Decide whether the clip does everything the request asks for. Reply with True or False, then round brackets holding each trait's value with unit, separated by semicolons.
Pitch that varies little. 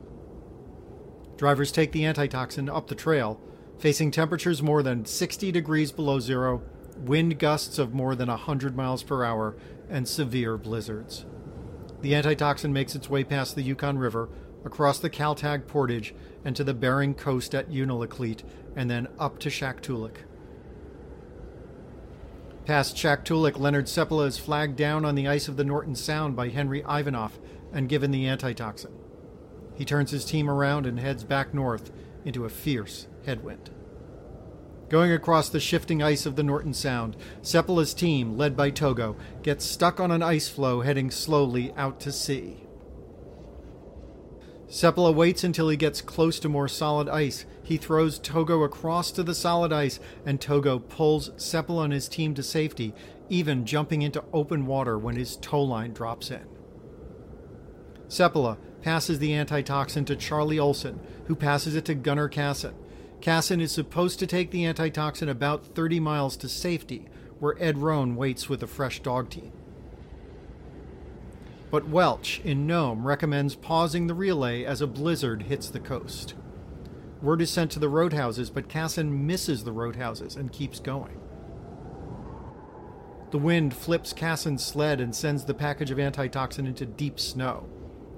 False (3.3 semitones)